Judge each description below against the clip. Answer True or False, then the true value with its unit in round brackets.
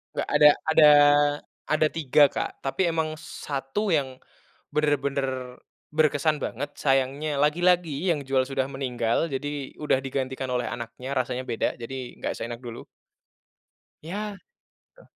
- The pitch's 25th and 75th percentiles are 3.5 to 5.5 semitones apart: False (2.9 semitones)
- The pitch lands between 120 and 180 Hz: True (140 Hz)